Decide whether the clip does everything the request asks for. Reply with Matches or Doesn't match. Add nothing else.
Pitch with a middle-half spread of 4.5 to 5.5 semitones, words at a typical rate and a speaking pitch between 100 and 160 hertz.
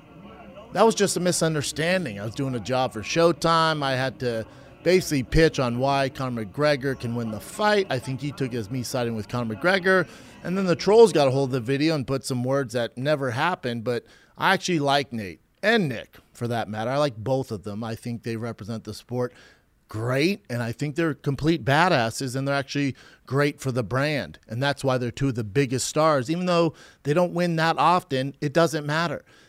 Doesn't match